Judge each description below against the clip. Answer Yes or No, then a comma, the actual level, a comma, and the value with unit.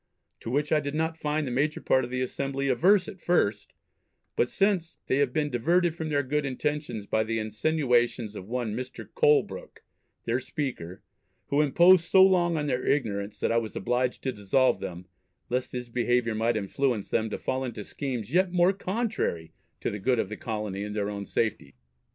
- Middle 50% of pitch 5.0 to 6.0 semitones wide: Yes, wide, 5.6 semitones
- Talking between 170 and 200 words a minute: Yes, average, 190 wpm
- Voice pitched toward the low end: Yes, low, 130 Hz